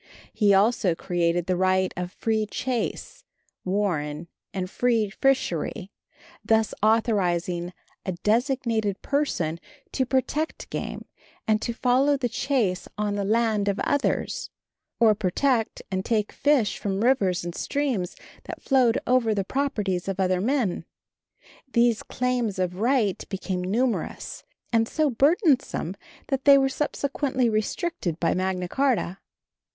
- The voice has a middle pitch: No, high, 215 Hz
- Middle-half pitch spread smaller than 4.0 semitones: No, wide, 5.5 semitones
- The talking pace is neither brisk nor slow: No, slow, 130 wpm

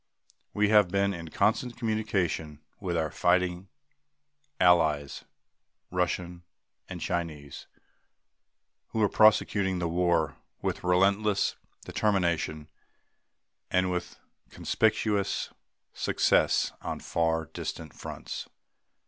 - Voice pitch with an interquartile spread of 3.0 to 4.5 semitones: Yes, average, 3.4 semitones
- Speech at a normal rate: No, slow, 90 wpm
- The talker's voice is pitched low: Yes, very low, 90 Hz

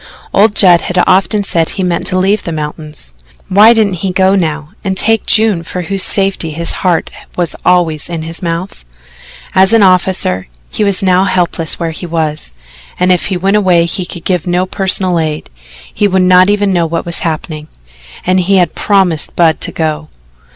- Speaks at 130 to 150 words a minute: No, average, 190 wpm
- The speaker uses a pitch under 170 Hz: No, medium, 180 Hz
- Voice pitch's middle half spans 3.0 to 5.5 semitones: No, narrow, 2.6 semitones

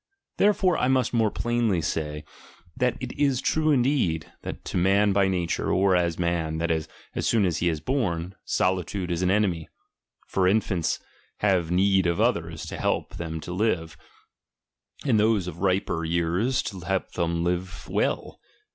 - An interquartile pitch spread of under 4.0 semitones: No, average, 4.6 semitones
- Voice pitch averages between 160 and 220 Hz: No, very low, 95 Hz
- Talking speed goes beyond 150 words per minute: Yes, average, 170 wpm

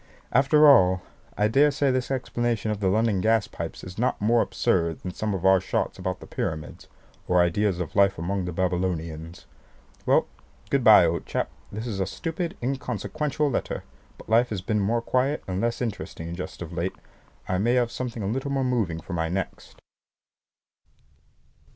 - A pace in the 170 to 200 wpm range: Yes, average, 175 wpm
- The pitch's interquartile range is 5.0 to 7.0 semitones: Yes, average, 5.3 semitones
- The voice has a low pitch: Yes, low, 105 Hz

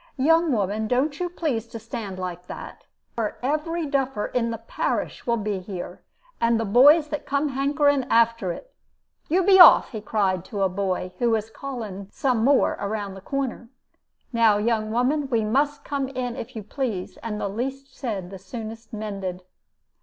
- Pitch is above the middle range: Yes, high, 230 Hz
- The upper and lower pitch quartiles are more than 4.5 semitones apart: Yes, average, 4.9 semitones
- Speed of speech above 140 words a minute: Yes, average, 180 wpm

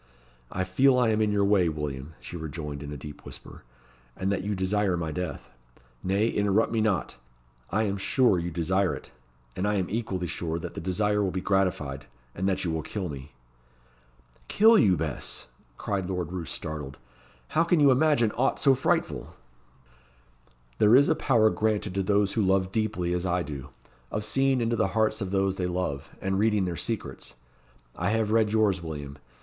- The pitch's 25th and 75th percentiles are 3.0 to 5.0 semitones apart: Yes, average, 3.8 semitones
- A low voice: Yes, very low, 95 Hz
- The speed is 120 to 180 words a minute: No, average, 190 wpm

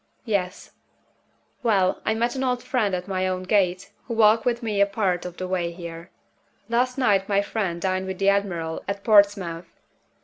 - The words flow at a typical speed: Yes, average, 180 wpm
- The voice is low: No, high, 200 Hz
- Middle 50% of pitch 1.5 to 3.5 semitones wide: Yes, average, 3.2 semitones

